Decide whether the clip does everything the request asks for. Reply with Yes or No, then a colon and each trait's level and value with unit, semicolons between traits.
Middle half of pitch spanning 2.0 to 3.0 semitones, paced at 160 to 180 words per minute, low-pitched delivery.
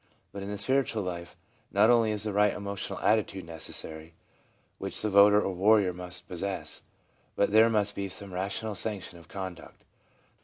Yes: narrow, 2.6 semitones; average, 165 wpm; low, 100 Hz